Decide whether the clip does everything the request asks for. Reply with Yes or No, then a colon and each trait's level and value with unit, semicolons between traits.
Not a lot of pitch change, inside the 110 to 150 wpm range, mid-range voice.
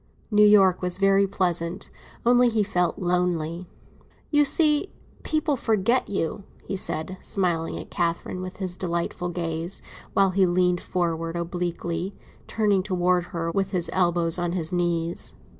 Yes: narrow, 2.3 semitones; average, 140 wpm; medium, 180 Hz